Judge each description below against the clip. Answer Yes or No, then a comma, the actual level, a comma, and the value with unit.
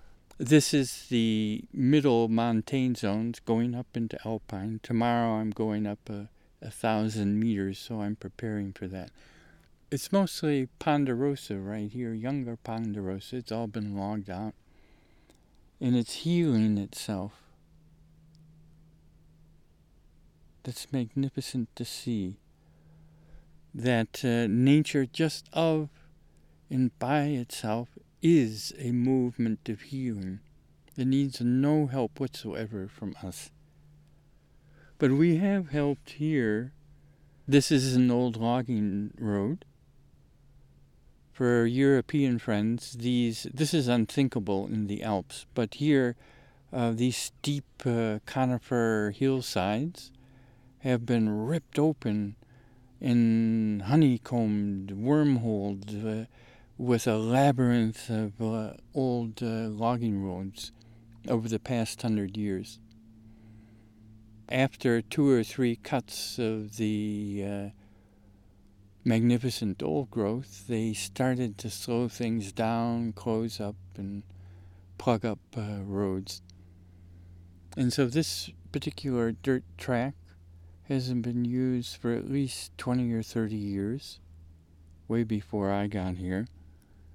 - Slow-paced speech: Yes, slow, 110 wpm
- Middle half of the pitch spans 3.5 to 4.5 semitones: Yes, average, 4.1 semitones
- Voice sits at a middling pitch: No, low, 115 Hz